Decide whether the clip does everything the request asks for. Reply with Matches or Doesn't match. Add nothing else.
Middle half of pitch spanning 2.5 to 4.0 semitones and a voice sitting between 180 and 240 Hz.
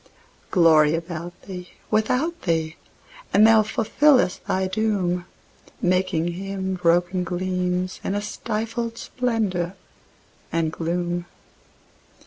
Matches